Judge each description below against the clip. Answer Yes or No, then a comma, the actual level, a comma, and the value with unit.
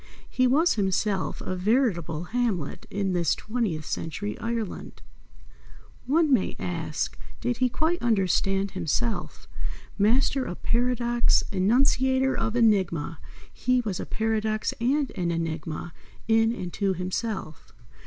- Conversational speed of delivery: No, slow, 120 wpm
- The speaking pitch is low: No, high, 215 Hz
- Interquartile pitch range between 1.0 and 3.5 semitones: No, average, 5.1 semitones